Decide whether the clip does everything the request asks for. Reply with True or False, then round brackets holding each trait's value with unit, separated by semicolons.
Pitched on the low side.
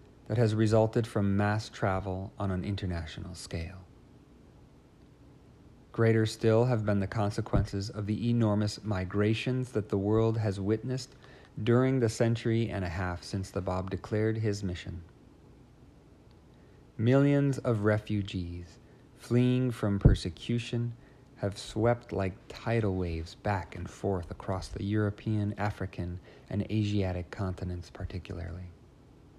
True (105 Hz)